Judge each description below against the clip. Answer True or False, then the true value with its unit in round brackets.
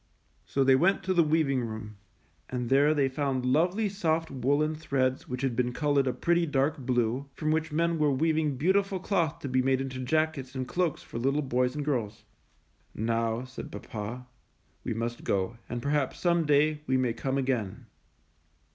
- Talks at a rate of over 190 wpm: False (180 wpm)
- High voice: False (135 Hz)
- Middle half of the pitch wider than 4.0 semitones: False (3.7 semitones)